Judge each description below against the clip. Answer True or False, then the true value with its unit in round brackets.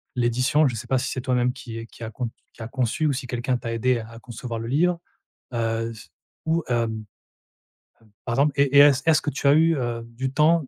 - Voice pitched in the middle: False (125 Hz)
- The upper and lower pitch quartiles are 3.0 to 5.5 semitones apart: True (3.4 semitones)